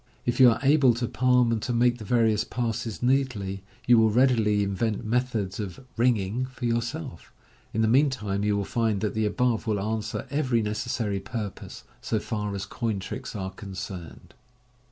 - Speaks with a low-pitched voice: Yes, low, 110 Hz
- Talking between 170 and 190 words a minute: Yes, average, 175 wpm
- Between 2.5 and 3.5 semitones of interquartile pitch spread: Yes, average, 3.1 semitones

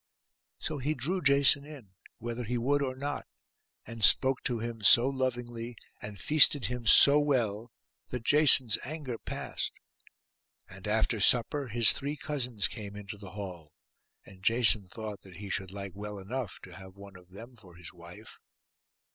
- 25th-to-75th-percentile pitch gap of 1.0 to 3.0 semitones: No, average, 4.8 semitones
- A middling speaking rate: Yes, average, 165 wpm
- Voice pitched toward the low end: Yes, low, 115 Hz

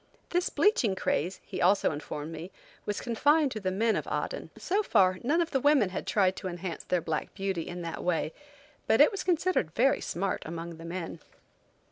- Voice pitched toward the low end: No, high, 190 Hz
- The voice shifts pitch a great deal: Yes, wide, 7.8 semitones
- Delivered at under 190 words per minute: No, average, 195 wpm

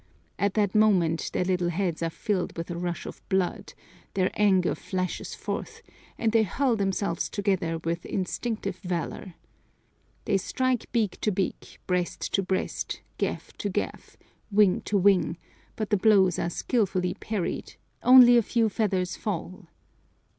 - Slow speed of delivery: No, average, 145 wpm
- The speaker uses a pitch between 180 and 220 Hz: Yes, high, 190 Hz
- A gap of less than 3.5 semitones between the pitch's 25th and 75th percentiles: Yes, average, 3.0 semitones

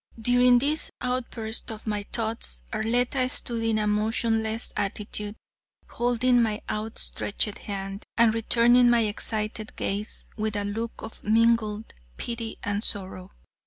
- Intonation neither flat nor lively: No, narrow, 1.9 semitones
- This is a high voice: Yes, high, 220 Hz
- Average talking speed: No, slow, 125 wpm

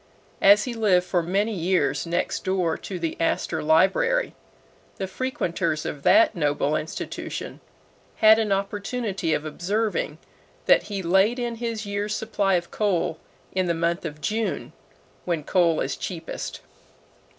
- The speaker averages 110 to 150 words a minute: Yes, average, 140 wpm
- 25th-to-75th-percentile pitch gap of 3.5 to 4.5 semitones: Yes, average, 4.2 semitones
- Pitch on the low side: No, high, 190 Hz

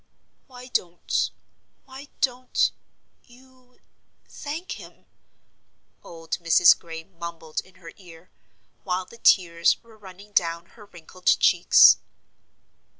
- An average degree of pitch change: No, wide, 6.7 semitones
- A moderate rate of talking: No, slow, 105 wpm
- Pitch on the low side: No, medium, 185 Hz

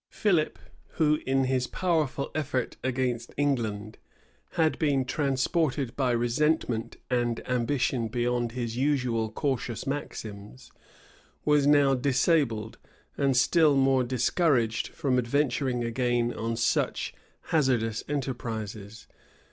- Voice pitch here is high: No, low, 125 Hz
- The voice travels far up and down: No, average, 3.4 semitones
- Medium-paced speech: No, slow, 105 wpm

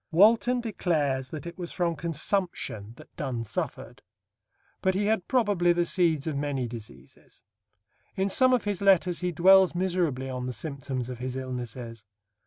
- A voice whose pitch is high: No, medium, 170 Hz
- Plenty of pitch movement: Yes, wide, 6.6 semitones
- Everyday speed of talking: Yes, average, 160 wpm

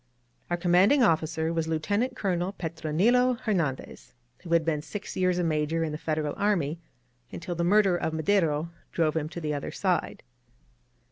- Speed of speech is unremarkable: Yes, average, 160 wpm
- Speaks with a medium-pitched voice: Yes, medium, 170 Hz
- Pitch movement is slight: No, average, 3.3 semitones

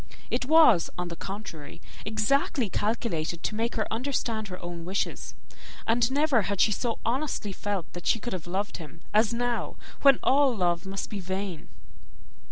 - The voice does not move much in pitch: No, average, 4.9 semitones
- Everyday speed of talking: Yes, average, 170 wpm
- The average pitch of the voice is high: Yes, high, 210 Hz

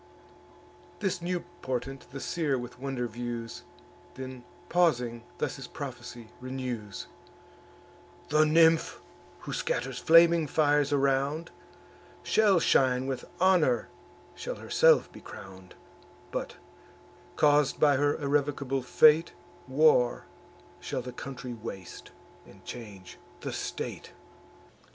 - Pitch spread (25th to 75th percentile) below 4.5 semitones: Yes, average, 4.0 semitones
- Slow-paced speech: Yes, slow, 105 wpm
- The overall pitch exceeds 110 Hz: Yes, low, 135 Hz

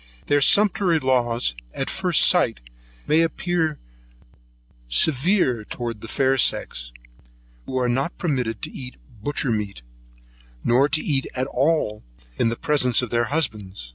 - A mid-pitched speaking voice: No, low, 130 Hz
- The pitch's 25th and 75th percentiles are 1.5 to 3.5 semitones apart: No, average, 4.5 semitones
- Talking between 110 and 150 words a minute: Yes, slow, 135 wpm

